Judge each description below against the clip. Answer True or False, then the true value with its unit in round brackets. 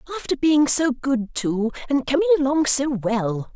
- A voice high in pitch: True (255 Hz)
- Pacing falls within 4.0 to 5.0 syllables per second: True (4.6 syllables/s)